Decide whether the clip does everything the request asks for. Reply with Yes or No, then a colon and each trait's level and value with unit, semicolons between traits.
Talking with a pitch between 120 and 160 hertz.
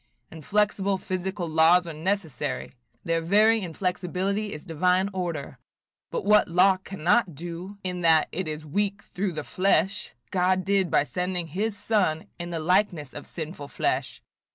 No: medium, 180 Hz